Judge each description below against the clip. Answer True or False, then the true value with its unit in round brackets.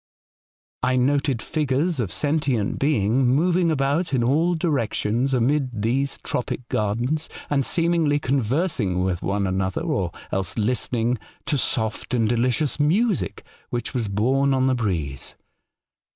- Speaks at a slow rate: True (130 wpm)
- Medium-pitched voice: False (130 Hz)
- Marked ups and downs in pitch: False (4.8 semitones)